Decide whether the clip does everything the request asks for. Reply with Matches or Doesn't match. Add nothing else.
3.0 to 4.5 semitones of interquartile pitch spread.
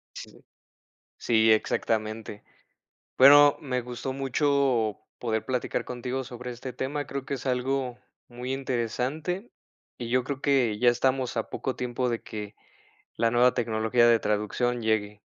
Doesn't match